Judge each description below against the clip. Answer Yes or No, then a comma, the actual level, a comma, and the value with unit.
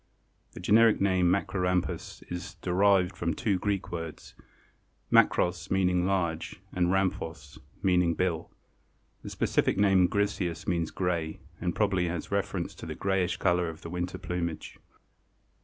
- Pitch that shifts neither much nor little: No, narrow, 1.8 semitones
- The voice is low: Yes, very low, 90 Hz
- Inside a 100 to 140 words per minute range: Yes, slow, 135 wpm